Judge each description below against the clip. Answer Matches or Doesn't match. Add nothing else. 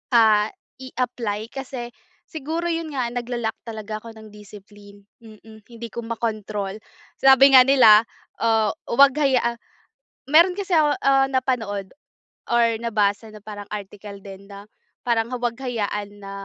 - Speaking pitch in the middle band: Doesn't match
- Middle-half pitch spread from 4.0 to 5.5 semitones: Doesn't match